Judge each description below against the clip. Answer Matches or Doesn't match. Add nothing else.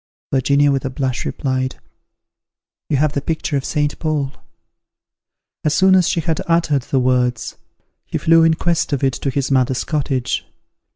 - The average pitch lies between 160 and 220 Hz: Doesn't match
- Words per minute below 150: Doesn't match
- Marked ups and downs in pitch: Doesn't match